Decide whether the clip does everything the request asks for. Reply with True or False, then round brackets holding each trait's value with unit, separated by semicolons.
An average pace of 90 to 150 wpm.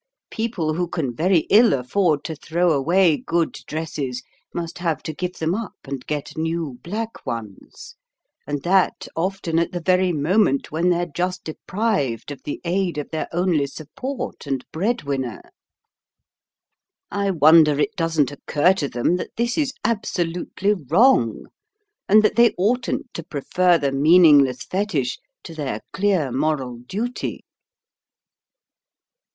True (140 wpm)